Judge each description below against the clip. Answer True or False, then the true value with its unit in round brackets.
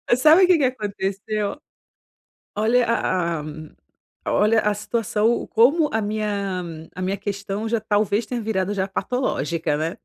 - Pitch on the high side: True (210 Hz)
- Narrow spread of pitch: False (3.0 semitones)